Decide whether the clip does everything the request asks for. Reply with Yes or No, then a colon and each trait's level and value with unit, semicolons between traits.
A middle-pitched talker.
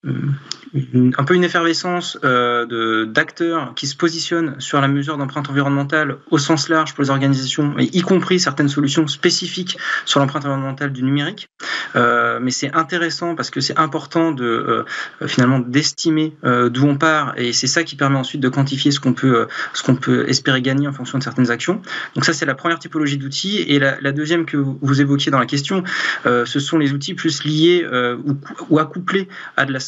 Yes: medium, 145 Hz